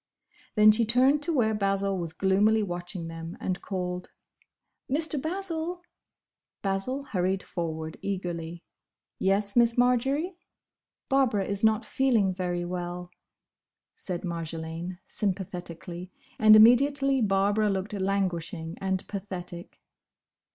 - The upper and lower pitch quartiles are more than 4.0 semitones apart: Yes, average, 4.7 semitones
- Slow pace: Yes, slow, 110 wpm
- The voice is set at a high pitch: Yes, high, 195 Hz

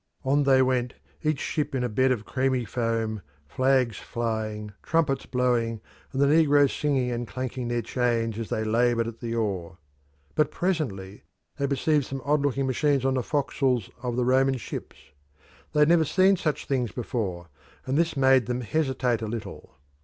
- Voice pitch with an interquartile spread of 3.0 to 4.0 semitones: Yes, average, 3.3 semitones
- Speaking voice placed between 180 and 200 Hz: No, low, 125 Hz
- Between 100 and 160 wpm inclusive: No, average, 175 wpm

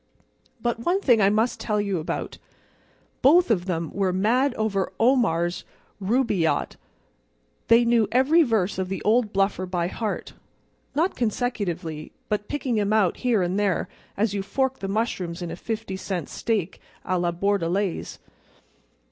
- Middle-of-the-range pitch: No, high, 205 Hz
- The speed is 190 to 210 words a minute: No, average, 145 wpm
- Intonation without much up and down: No, average, 4.2 semitones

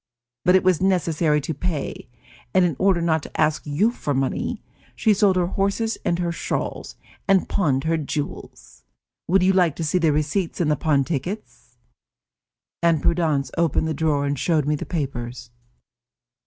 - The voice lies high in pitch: No, medium, 165 Hz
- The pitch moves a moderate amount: Yes, average, 3.6 semitones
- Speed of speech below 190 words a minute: Yes, average, 170 wpm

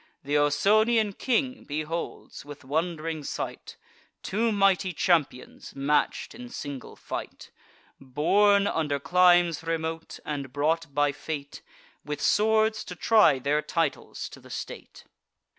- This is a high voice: No, medium, 165 Hz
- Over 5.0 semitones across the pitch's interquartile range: Yes, wide, 5.5 semitones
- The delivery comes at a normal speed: No, slow, 120 wpm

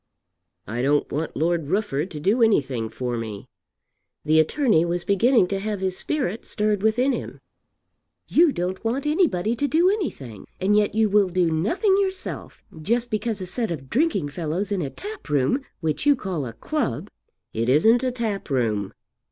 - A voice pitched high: Yes, high, 195 Hz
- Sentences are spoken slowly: No, average, 175 wpm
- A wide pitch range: Yes, wide, 8.0 semitones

